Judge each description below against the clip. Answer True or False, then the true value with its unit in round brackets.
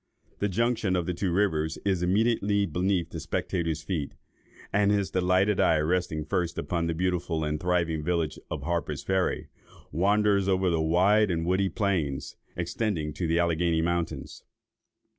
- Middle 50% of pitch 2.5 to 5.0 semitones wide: True (3.1 semitones)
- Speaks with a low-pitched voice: True (90 Hz)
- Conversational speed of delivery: True (155 wpm)